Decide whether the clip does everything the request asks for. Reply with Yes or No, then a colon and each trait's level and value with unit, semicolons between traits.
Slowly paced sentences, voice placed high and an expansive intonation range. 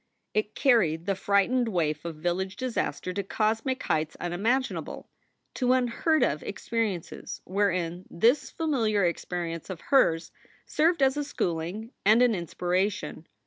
Yes: slow, 130 wpm; high, 200 Hz; wide, 6.0 semitones